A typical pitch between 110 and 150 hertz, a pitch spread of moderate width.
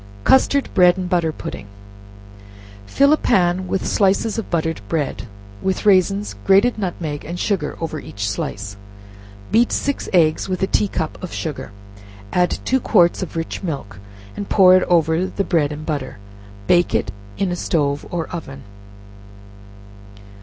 No: medium, 175 Hz; average, 3.9 semitones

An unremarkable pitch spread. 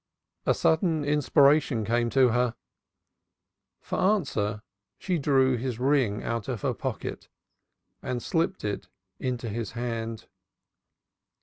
Yes: average, 4.1 semitones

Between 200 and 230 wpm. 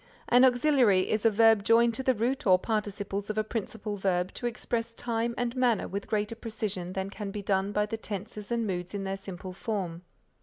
Yes: fast, 205 wpm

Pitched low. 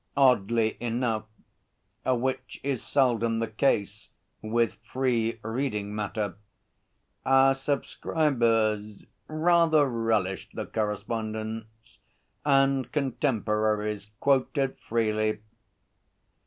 Yes: low, 115 Hz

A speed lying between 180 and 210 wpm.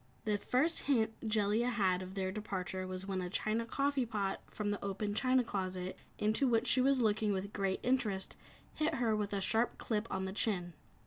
Yes: average, 190 wpm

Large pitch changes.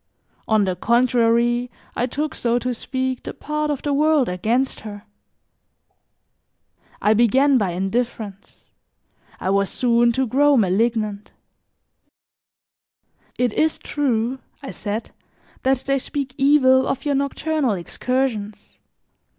No: average, 3.8 semitones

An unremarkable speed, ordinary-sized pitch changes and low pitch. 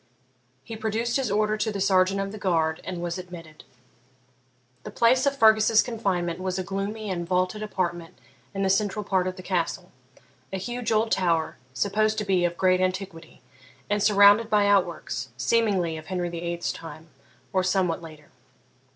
No: average, 170 wpm; average, 3.5 semitones; high, 190 Hz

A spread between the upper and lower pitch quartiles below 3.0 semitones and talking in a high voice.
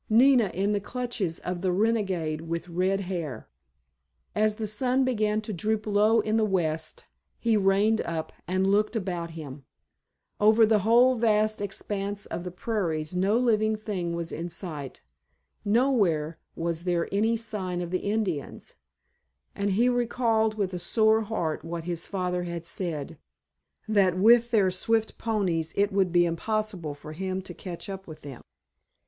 No: average, 4.1 semitones; high, 195 Hz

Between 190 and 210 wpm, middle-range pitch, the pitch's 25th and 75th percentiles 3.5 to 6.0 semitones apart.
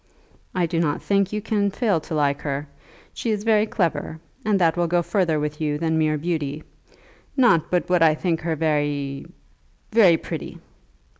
No: average, 175 wpm; medium, 165 Hz; average, 4.4 semitones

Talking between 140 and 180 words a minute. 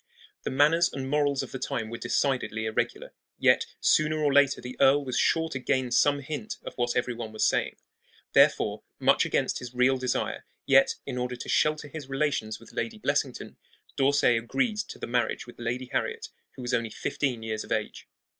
No: average, 190 wpm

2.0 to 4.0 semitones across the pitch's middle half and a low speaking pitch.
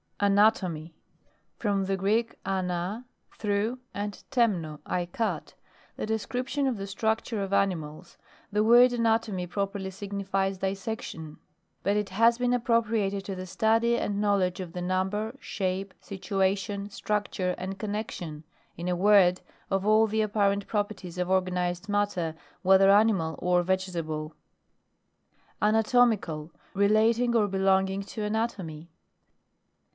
No: average, 2.8 semitones; high, 200 Hz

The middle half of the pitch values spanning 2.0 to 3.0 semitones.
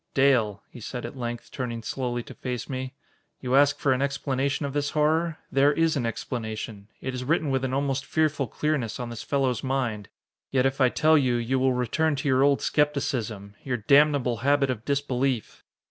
Yes: average, 2.7 semitones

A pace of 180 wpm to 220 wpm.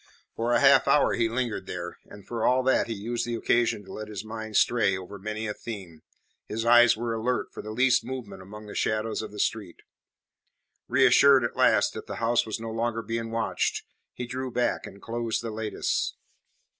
Yes: average, 200 wpm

